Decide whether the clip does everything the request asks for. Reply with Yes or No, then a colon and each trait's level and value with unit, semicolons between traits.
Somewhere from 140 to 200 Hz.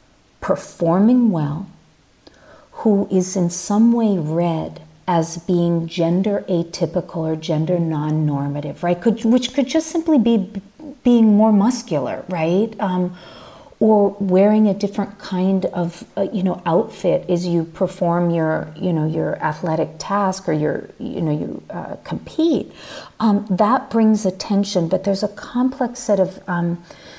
Yes: medium, 185 Hz